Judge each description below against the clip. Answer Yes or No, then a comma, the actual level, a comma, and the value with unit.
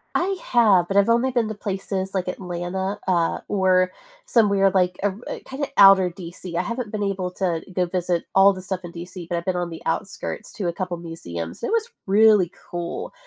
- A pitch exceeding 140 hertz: Yes, high, 190 Hz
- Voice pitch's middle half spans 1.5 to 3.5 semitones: Yes, narrow, 2.4 semitones